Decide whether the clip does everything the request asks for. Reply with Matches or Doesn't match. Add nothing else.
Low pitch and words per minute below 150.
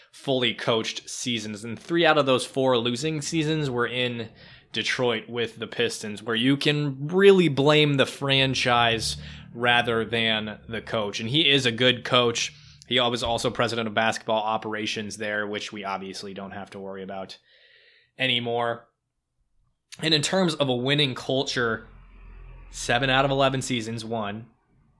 Doesn't match